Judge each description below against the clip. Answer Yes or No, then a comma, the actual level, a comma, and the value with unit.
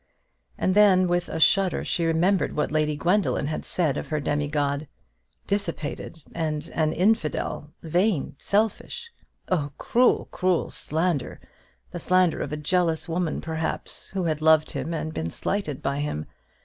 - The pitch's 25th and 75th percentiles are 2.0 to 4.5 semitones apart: Yes, average, 3.4 semitones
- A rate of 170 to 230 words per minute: No, average, 150 wpm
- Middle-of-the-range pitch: Yes, medium, 160 Hz